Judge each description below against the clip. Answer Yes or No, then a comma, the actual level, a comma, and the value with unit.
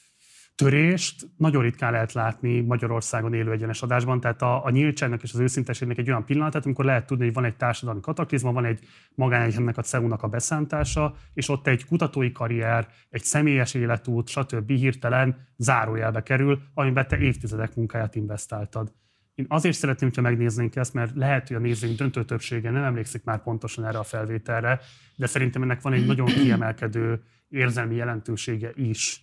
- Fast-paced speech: Yes, fast, 165 wpm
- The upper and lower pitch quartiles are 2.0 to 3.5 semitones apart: Yes, narrow, 2.5 semitones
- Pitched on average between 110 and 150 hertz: Yes, low, 120 Hz